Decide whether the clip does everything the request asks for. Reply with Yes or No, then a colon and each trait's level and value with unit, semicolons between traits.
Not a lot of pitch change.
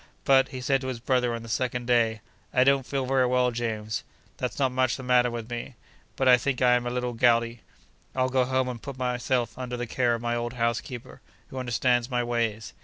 Yes: narrow, 1.5 semitones